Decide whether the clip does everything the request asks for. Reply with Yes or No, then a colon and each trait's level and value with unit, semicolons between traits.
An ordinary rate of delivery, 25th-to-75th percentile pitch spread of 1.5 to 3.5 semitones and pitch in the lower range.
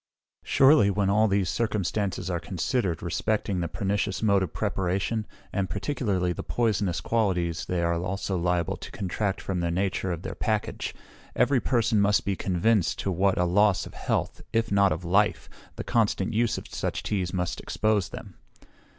Yes: average, 170 wpm; average, 3.2 semitones; low, 100 Hz